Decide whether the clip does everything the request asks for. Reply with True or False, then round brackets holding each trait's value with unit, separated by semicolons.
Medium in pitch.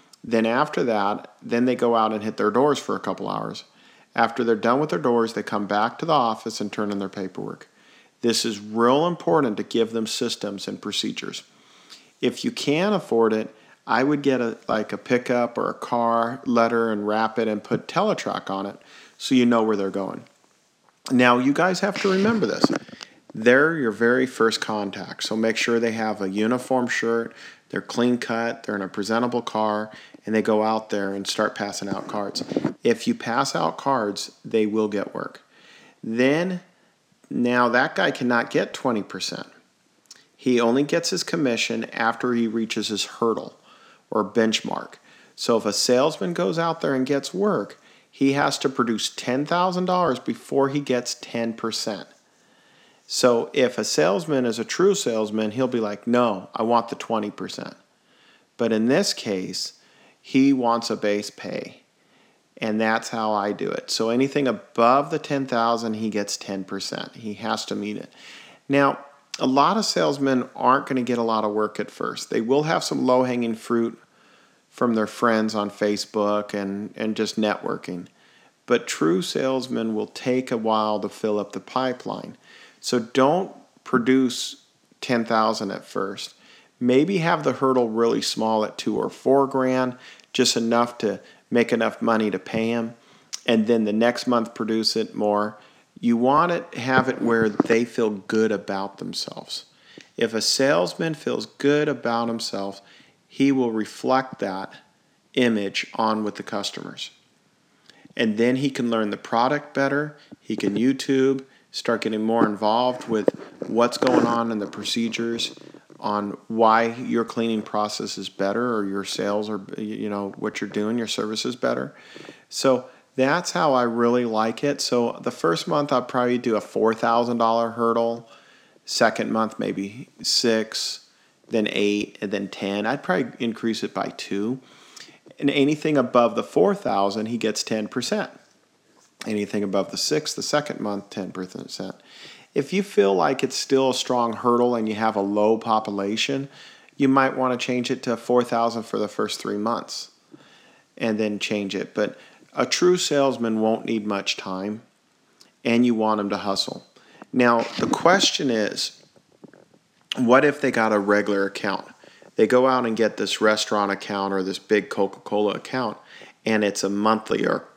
False (115 Hz)